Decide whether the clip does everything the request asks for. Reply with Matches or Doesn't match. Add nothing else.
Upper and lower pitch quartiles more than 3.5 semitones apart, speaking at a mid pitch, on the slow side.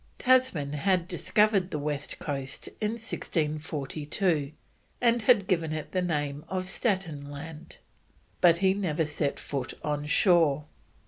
Matches